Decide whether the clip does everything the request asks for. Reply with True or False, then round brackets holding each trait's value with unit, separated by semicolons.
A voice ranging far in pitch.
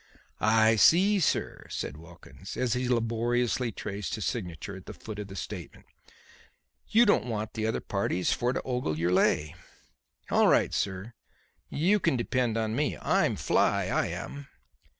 False (4.2 semitones)